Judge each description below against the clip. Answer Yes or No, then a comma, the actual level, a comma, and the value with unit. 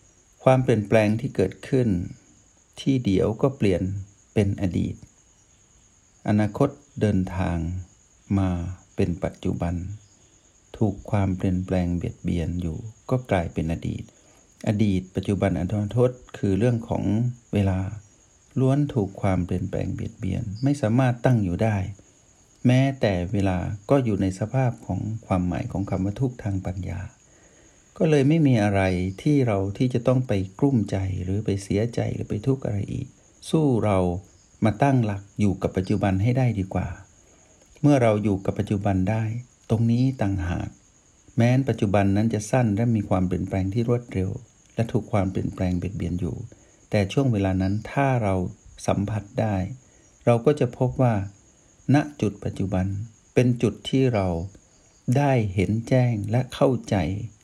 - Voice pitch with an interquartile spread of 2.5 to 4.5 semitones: Yes, average, 4.2 semitones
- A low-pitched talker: Yes, low, 105 Hz